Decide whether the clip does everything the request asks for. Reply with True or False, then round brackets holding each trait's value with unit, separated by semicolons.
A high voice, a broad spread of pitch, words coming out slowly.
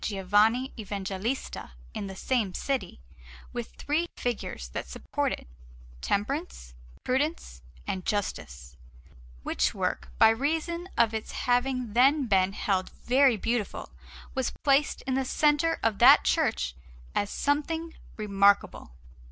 True (230 Hz; 5.8 semitones; 120 wpm)